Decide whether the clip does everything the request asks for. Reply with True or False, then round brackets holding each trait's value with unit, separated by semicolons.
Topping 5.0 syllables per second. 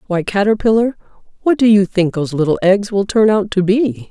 True (5.5 syllables/s)